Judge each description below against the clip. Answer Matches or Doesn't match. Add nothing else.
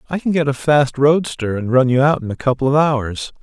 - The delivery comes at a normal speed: Doesn't match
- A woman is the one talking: Doesn't match